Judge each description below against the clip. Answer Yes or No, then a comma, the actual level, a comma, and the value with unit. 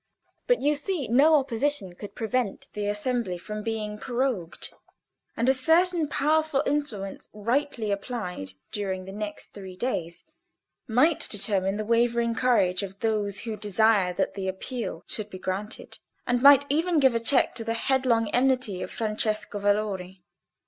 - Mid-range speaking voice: No, high, 225 Hz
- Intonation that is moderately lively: Yes, average, 4.5 semitones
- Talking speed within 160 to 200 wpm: No, average, 150 wpm